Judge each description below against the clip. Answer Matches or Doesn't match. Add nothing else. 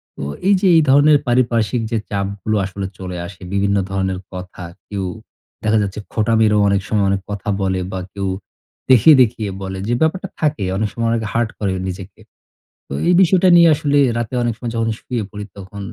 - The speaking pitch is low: Matches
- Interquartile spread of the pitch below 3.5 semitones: Doesn't match